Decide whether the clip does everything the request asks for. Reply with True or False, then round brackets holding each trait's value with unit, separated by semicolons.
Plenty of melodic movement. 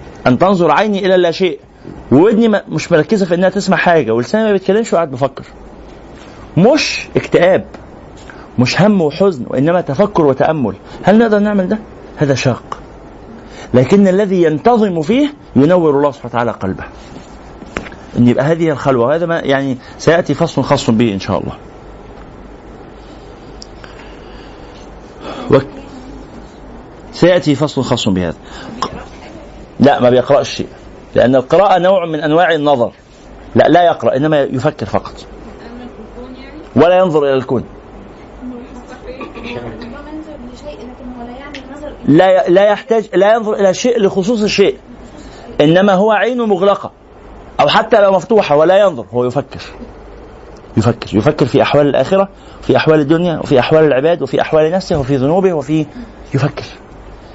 True (7.0 semitones)